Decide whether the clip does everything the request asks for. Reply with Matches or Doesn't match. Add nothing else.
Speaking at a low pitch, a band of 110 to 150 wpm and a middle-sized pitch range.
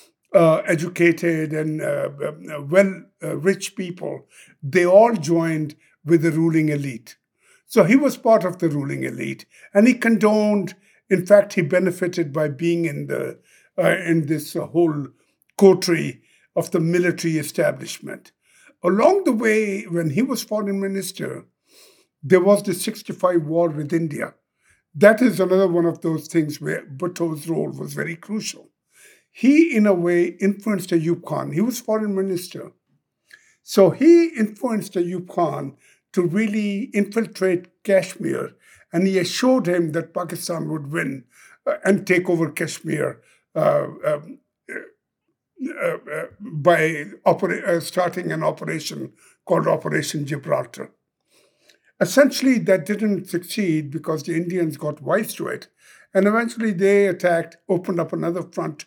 Doesn't match